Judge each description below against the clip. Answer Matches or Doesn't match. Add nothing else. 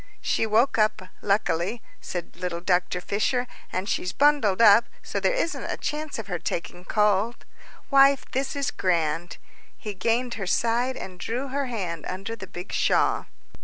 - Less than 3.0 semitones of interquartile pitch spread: Doesn't match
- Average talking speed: Matches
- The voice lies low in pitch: Doesn't match